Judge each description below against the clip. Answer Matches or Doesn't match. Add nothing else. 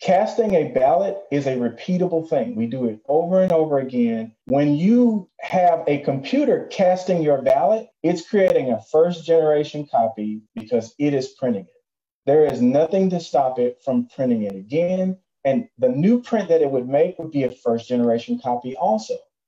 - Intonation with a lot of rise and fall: Matches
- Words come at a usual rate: Matches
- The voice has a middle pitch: Matches